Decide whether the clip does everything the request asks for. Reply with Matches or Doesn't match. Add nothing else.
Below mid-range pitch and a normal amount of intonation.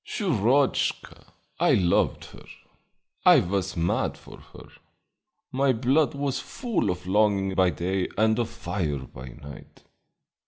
Doesn't match